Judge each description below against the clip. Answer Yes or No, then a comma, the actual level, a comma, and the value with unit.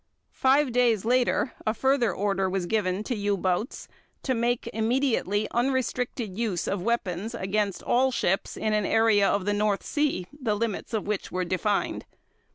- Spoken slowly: No, average, 165 wpm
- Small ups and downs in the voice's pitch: No, average, 3.6 semitones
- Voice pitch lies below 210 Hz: No, high, 215 Hz